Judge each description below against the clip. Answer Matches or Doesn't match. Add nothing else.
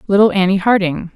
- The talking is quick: Doesn't match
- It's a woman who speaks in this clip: Matches